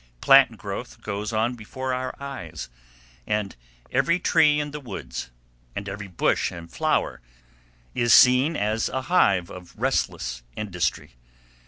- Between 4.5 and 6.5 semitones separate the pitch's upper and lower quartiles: Yes, wide, 5.4 semitones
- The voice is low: Yes, low, 110 Hz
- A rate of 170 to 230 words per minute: No, slow, 135 wpm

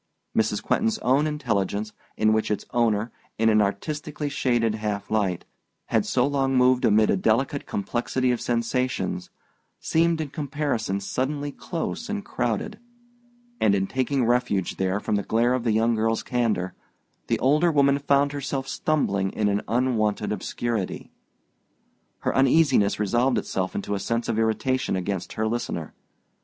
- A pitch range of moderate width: Yes, average, 4.6 semitones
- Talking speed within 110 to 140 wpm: No, average, 150 wpm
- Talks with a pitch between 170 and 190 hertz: No, low, 120 Hz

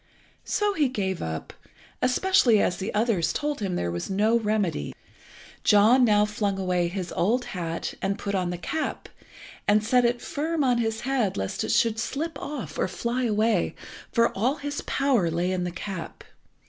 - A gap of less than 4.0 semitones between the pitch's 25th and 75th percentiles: No, average, 5.2 semitones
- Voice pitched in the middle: No, high, 215 Hz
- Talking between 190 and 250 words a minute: No, average, 175 wpm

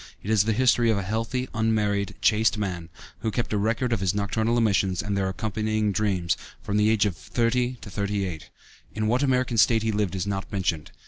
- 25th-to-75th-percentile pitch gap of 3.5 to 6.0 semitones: No, narrow, 2.4 semitones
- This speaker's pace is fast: Yes, fast, 210 wpm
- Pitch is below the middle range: Yes, low, 105 Hz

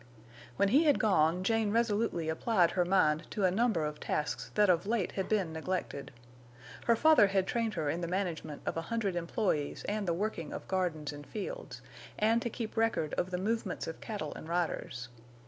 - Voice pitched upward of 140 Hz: Yes, high, 190 Hz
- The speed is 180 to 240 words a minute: Yes, average, 195 wpm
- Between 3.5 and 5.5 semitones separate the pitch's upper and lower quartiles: Yes, average, 5.1 semitones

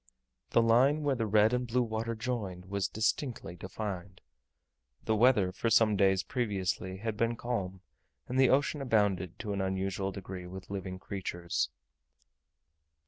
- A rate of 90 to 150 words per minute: Yes, average, 145 wpm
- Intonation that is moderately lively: Yes, average, 3.6 semitones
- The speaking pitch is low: Yes, low, 105 Hz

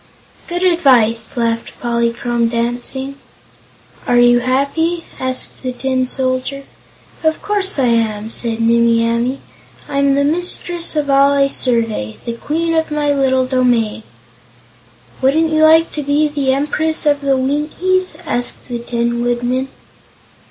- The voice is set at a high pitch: Yes, very high, 265 Hz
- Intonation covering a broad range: No, average, 3.9 semitones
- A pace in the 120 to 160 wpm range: Yes, slow, 135 wpm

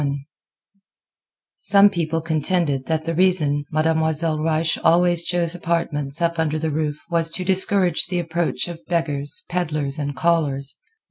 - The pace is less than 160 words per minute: Yes, average, 140 wpm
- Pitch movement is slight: Yes, narrow, 2.3 semitones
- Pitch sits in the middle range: Yes, medium, 165 Hz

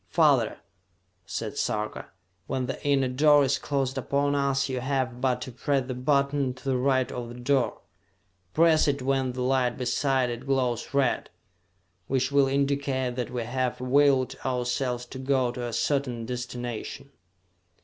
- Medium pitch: No, low, 130 Hz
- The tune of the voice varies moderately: No, narrow, 1.9 semitones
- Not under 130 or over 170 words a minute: Yes, average, 160 wpm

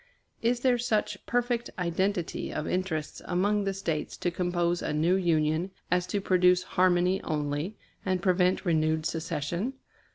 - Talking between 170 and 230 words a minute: No, average, 140 wpm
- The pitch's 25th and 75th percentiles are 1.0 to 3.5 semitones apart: Yes, average, 3.1 semitones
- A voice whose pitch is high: No, medium, 180 Hz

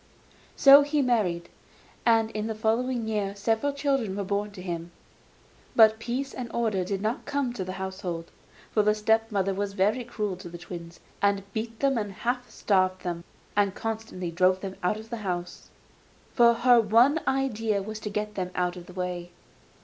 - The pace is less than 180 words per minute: No, average, 185 wpm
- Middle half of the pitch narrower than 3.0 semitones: No, average, 3.7 semitones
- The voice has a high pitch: Yes, high, 210 Hz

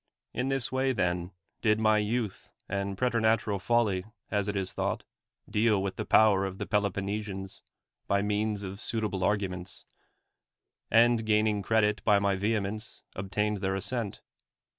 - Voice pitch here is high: No, low, 105 Hz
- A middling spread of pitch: No, narrow, 2.1 semitones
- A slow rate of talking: No, average, 155 wpm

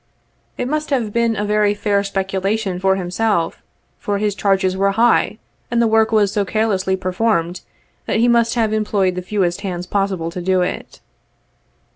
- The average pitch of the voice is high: Yes, high, 200 Hz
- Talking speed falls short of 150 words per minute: No, average, 175 wpm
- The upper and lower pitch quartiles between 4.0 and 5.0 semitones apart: No, average, 2.7 semitones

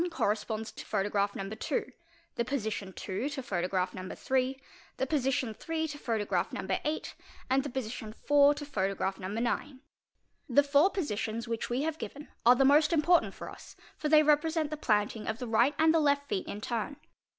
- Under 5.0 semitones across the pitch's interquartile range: No, wide, 5.4 semitones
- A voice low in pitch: No, very high, 255 Hz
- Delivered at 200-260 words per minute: No, average, 185 wpm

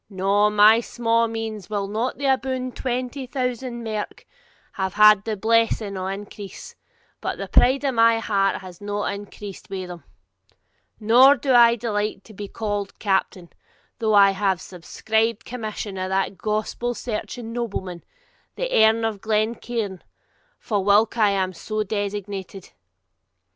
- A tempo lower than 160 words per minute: Yes, average, 145 wpm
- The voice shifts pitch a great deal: No, average, 2.7 semitones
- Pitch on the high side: Yes, high, 215 Hz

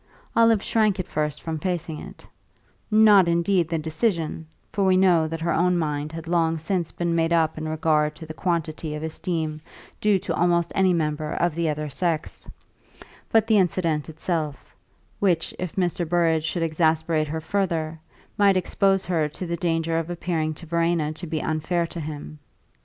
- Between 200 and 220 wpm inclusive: No, average, 175 wpm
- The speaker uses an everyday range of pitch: No, narrow, 2.3 semitones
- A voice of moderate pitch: Yes, medium, 165 Hz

